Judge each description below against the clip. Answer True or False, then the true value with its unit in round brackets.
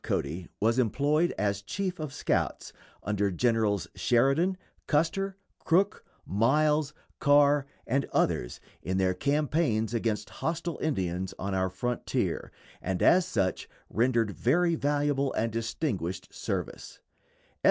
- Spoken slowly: True (115 wpm)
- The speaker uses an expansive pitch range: True (7.1 semitones)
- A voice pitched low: True (125 Hz)